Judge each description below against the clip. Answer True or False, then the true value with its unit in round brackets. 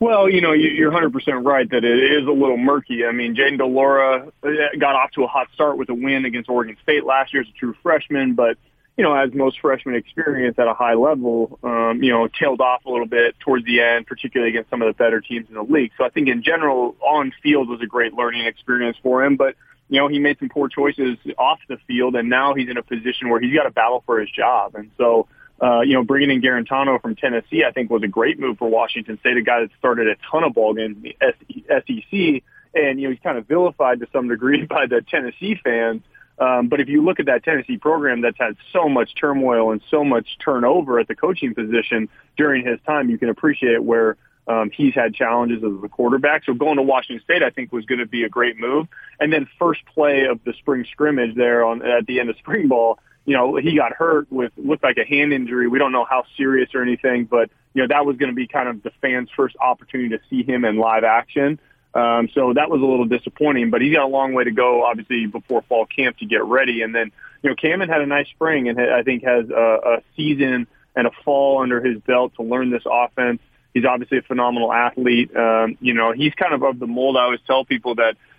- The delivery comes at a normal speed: False (245 wpm)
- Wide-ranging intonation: False (3.0 semitones)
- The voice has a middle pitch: False (125 Hz)